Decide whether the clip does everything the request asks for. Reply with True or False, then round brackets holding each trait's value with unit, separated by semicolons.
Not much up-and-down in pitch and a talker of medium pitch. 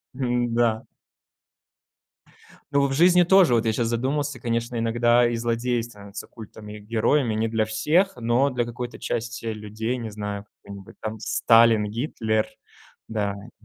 False (2.0 semitones; 115 Hz)